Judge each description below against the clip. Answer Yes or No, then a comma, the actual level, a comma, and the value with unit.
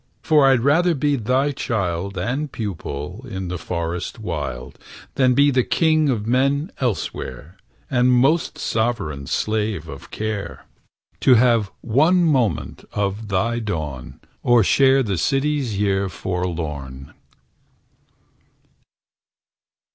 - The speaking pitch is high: No, low, 110 Hz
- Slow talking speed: Yes, slow, 115 wpm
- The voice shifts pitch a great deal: Yes, wide, 6.9 semitones